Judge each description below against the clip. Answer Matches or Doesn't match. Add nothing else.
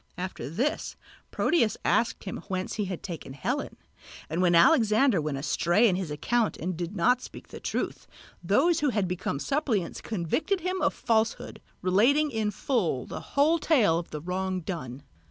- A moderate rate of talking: Matches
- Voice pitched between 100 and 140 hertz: Doesn't match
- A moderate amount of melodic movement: Doesn't match